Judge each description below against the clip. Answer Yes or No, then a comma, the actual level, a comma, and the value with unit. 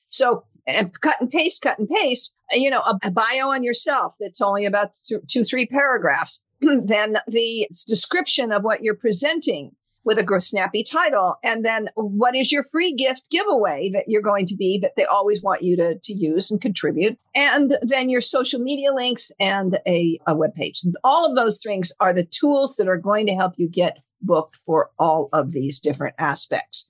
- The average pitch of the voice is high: Yes, high, 215 Hz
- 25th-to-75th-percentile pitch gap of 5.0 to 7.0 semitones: Yes, average, 5.3 semitones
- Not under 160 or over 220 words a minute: Yes, average, 200 wpm